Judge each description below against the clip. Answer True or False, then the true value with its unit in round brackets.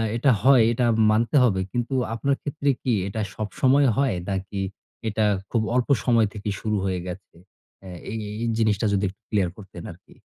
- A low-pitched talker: True (110 Hz)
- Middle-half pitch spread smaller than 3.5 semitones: False (3.9 semitones)